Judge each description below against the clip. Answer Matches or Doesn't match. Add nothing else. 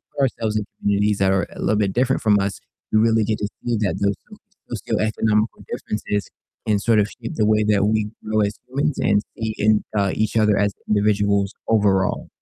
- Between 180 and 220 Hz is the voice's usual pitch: Doesn't match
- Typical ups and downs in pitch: Doesn't match